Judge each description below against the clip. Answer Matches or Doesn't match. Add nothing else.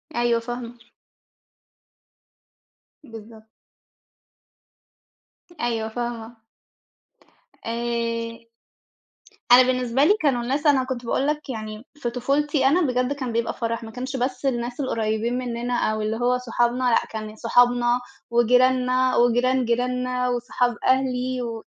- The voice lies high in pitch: Matches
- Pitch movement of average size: Doesn't match